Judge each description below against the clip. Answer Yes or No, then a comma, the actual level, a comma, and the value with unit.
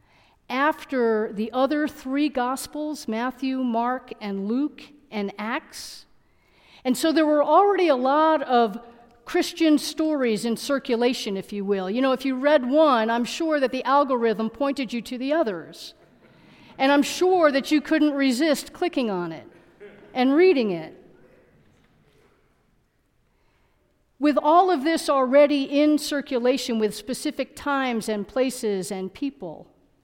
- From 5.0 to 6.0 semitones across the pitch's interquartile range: No, average, 4.5 semitones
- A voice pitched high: Yes, very high, 265 Hz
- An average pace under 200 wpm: Yes, average, 140 wpm